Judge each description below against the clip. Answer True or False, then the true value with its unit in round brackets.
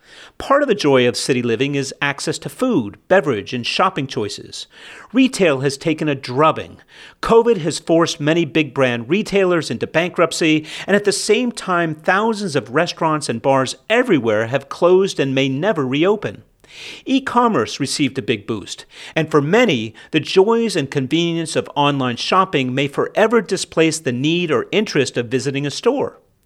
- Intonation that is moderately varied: False (5.8 semitones)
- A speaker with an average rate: True (165 wpm)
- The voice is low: False (160 Hz)